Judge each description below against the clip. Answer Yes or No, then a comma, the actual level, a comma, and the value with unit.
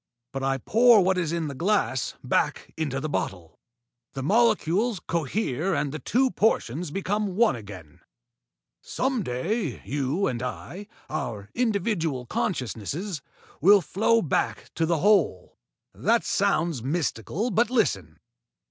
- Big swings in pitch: Yes, wide, 7.7 semitones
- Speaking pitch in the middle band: Yes, medium, 170 Hz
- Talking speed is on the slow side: Yes, slow, 130 wpm